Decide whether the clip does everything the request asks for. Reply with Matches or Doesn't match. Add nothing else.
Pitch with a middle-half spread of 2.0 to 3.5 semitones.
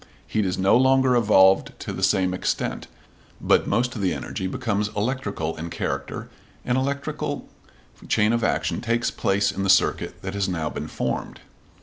Doesn't match